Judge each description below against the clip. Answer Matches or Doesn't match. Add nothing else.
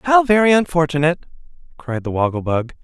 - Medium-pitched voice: Matches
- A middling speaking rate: Matches